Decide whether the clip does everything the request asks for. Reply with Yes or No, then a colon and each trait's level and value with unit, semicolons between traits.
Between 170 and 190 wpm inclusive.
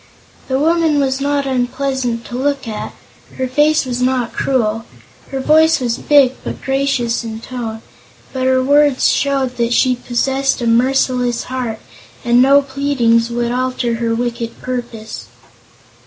No: average, 145 wpm